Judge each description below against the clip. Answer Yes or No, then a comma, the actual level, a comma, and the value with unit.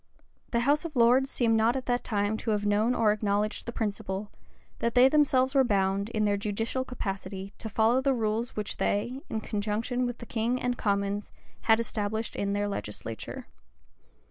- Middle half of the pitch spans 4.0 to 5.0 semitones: No, average, 3.2 semitones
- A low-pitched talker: No, high, 220 Hz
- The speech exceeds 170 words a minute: Yes, average, 180 wpm